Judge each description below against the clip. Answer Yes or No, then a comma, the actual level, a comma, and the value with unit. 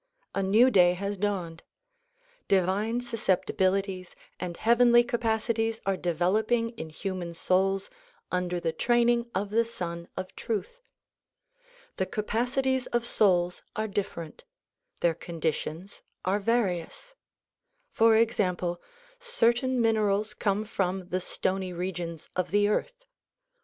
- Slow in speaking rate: Yes, slow, 115 wpm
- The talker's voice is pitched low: No, high, 200 Hz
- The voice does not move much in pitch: No, average, 4.1 semitones